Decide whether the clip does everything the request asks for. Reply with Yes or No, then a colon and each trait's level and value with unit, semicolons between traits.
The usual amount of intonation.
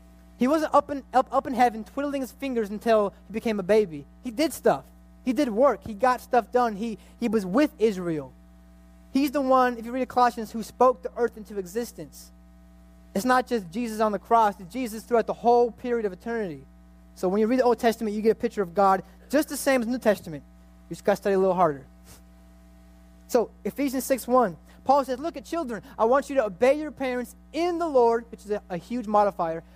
No: wide, 5.7 semitones